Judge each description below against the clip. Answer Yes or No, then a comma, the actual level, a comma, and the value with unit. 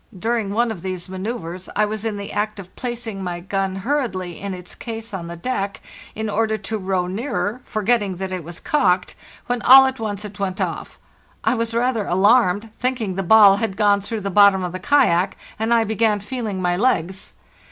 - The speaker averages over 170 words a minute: Yes, average, 200 wpm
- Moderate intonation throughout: Yes, average, 3.3 semitones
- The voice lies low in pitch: No, high, 205 Hz